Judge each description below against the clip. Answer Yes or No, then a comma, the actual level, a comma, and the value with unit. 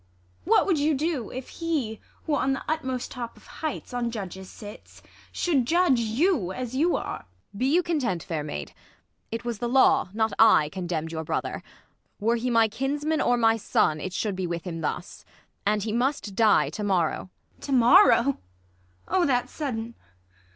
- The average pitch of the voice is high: Yes, high, 235 Hz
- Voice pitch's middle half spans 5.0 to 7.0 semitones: Yes, wide, 5.4 semitones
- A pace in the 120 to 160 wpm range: No, average, 185 wpm